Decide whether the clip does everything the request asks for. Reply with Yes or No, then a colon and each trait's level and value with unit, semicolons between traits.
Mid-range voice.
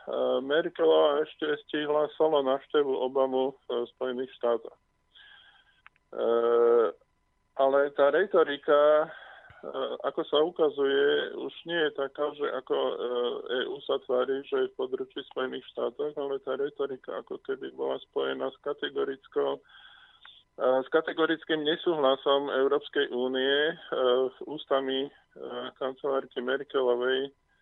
Yes: medium, 160 Hz